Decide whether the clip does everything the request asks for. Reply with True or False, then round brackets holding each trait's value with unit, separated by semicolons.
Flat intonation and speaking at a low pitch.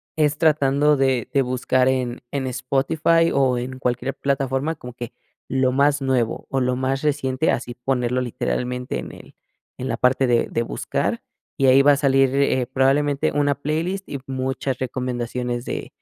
True (2.0 semitones; 130 Hz)